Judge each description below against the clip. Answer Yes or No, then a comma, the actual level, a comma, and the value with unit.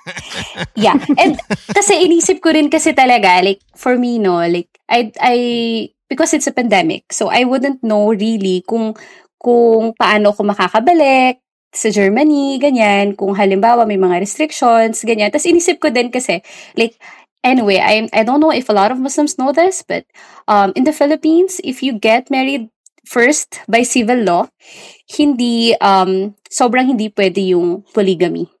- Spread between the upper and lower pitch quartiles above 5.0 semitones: Yes, wide, 5.6 semitones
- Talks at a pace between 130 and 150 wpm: No, average, 160 wpm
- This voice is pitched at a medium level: No, high, 240 Hz